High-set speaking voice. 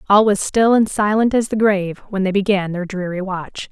Yes: high, 200 Hz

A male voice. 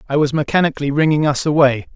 Yes: male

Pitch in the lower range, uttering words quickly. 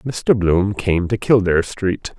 No: low, 100 Hz; average, 165 wpm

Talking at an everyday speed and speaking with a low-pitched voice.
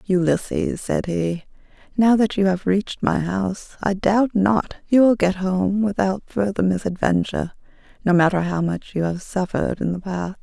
No: average, 175 wpm; high, 190 Hz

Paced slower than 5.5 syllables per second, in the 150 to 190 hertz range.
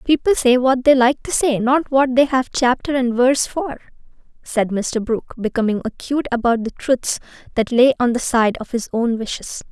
No: 5.1 syllables/s; very high, 250 Hz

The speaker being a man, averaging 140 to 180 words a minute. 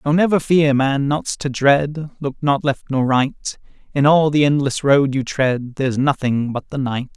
No: male; average, 200 wpm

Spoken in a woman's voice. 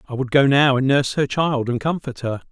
No: male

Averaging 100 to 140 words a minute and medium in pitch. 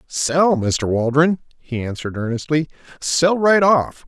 Yes: slow, 135 wpm; medium, 145 Hz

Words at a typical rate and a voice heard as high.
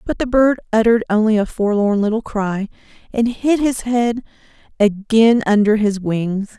Yes: average, 155 wpm; high, 220 Hz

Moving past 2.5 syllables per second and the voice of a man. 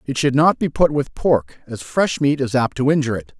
Yes: 5.3 syllables/s; male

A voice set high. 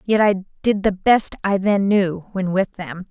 Yes: high, 195 Hz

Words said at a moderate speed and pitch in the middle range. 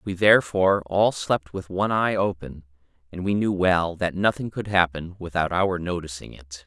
No: average, 180 wpm; very low, 90 Hz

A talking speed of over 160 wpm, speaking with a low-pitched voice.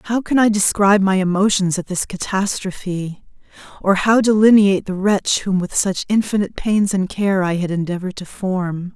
No: average, 175 wpm; high, 195 Hz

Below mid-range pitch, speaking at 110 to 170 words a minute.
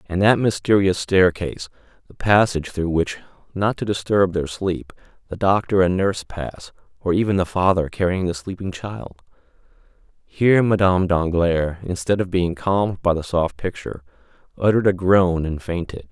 Yes: very low, 90 Hz; average, 155 wpm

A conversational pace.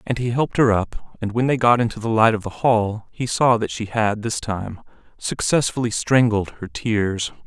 No: fast, 210 wpm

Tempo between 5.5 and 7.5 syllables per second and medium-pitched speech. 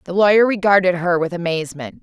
Yes: 6.4 syllables/s; medium, 180 Hz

